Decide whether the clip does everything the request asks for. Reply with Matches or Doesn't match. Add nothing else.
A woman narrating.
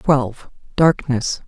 Matches